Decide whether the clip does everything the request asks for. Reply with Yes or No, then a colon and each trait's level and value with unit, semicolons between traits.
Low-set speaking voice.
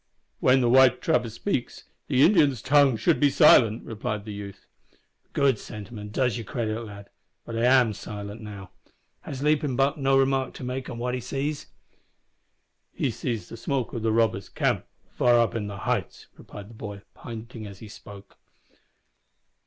Yes: low, 120 Hz